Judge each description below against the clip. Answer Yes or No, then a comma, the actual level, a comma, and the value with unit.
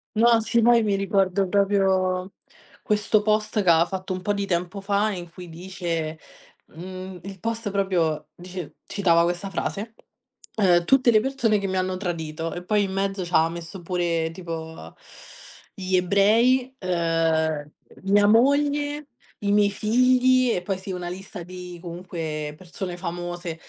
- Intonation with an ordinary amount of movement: Yes, average, 3.1 semitones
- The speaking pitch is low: No, medium, 185 Hz